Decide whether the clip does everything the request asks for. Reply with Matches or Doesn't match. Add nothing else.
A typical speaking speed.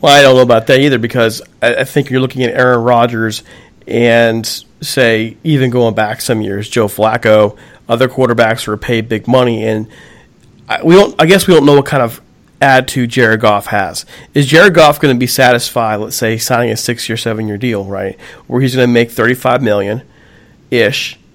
Matches